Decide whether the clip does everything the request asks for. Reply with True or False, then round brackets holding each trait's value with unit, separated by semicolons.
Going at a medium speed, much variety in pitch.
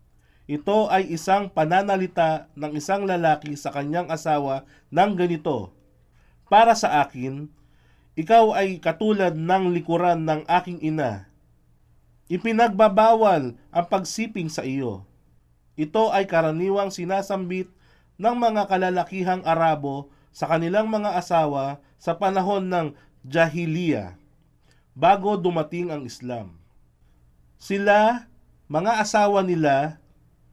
False (100 wpm; 5.8 semitones)